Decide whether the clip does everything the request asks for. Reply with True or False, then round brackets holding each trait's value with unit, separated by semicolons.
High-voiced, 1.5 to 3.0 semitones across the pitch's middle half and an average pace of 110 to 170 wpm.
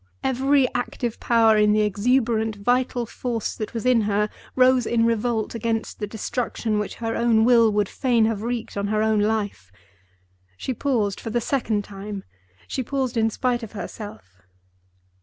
True (225 Hz; 2.6 semitones; 165 wpm)